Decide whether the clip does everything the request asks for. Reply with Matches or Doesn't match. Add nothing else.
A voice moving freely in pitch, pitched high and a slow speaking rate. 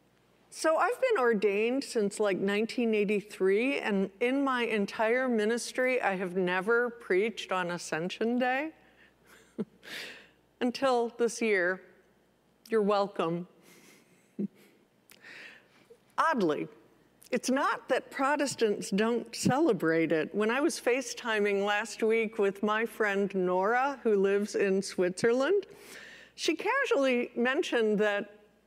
Doesn't match